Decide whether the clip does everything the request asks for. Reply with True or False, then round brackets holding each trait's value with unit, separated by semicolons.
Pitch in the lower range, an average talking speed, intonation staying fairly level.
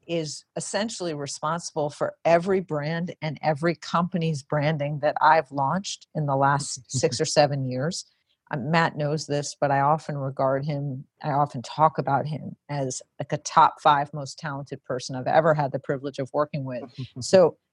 False (150 Hz; 170 wpm; 2.3 semitones)